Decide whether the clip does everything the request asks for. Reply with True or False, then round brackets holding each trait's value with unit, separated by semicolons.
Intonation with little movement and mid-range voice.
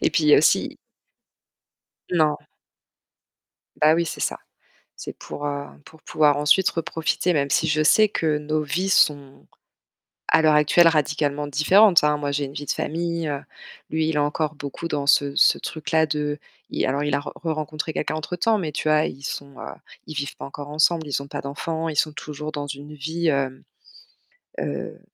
True (1.8 semitones; 150 Hz)